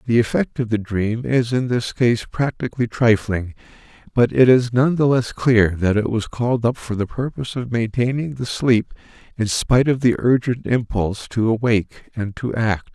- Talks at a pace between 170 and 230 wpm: Yes, average, 190 wpm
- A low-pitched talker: Yes, low, 115 Hz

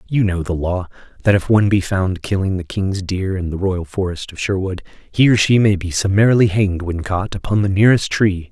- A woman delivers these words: No, male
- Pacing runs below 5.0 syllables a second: No, 5.5 syllables/s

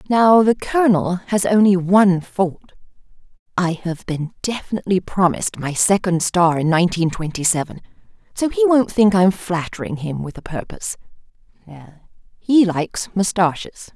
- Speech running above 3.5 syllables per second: No, 2.6 syllables/s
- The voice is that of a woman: Yes, female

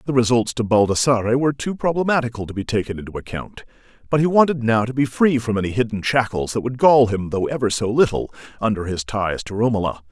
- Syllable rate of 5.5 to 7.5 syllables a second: Yes, 6.3 syllables/s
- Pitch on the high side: No, low, 120 Hz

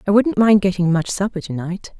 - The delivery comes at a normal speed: No, fast, 210 wpm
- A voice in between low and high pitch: No, high, 195 Hz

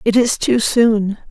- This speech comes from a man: No, female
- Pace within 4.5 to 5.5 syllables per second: No, 3.6 syllables/s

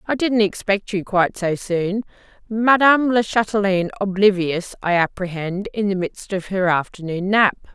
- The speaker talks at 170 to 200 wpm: No, average, 155 wpm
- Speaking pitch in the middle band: No, high, 195 Hz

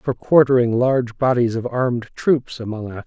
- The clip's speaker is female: No, male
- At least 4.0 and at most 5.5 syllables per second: Yes, 5.1 syllables/s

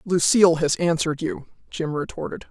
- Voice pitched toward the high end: No, medium, 170 Hz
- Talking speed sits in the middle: Yes, average, 145 wpm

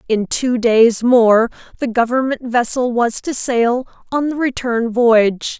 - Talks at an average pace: Yes, average, 150 wpm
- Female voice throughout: Yes, female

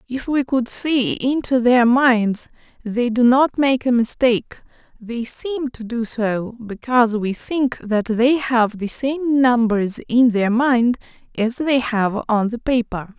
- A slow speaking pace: No, average, 165 wpm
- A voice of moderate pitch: No, high, 240 Hz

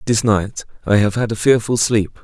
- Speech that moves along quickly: Yes, fast, 215 wpm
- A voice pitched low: Yes, low, 110 Hz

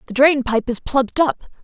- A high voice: Yes, very high, 260 Hz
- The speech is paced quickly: Yes, fast, 220 wpm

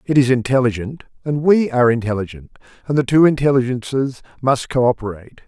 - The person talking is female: No, male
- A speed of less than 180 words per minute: Yes, average, 140 wpm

